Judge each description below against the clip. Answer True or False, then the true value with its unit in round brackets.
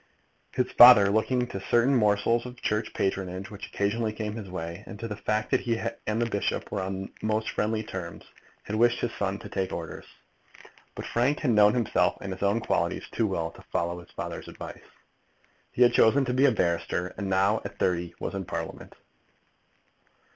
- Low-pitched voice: True (105 Hz)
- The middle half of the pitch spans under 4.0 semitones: True (3.4 semitones)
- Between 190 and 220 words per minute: True (195 wpm)